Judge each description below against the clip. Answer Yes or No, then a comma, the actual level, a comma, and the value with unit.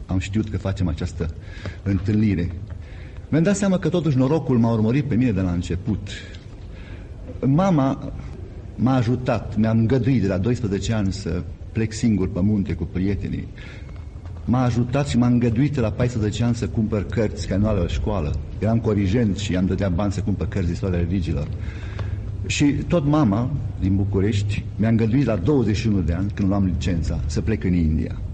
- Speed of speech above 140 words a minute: Yes, fast, 170 wpm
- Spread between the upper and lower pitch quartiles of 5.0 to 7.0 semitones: No, average, 3.7 semitones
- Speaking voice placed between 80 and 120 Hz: Yes, low, 100 Hz